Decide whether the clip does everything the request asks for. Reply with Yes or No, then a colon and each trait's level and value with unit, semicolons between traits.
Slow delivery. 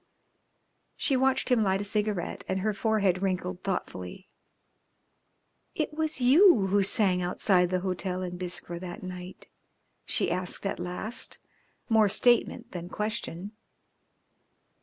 Yes: slow, 125 wpm